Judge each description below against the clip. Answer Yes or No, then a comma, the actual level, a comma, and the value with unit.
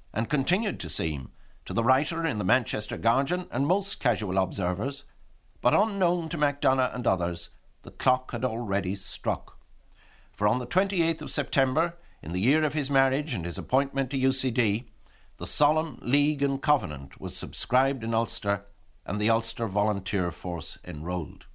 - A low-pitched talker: Yes, low, 125 Hz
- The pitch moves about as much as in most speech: No, wide, 6.5 semitones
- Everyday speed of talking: Yes, average, 160 wpm